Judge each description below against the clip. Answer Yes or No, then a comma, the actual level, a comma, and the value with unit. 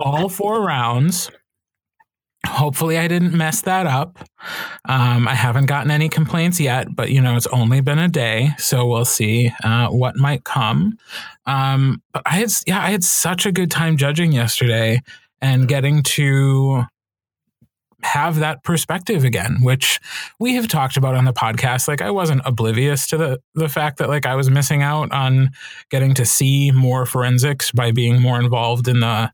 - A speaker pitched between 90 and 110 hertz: No, low, 135 Hz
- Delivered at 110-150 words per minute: No, average, 175 wpm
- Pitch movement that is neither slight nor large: Yes, average, 4.3 semitones